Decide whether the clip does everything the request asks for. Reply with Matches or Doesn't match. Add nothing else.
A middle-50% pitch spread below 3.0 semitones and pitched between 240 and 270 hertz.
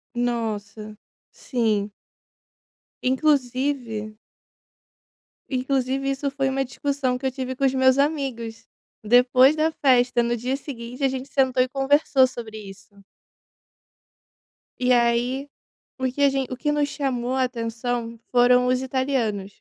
Matches